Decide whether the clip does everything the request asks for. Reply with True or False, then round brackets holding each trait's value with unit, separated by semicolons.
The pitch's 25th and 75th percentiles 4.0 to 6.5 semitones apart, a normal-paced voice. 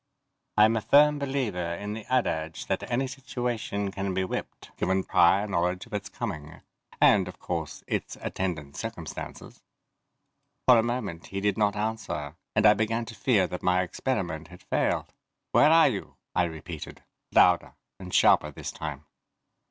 True (4.7 semitones; 160 wpm)